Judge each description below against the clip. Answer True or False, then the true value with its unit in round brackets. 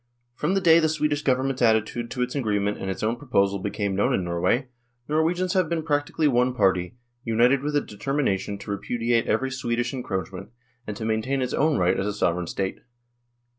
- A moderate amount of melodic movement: False (6.0 semitones)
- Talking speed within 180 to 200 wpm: True (190 wpm)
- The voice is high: False (120 Hz)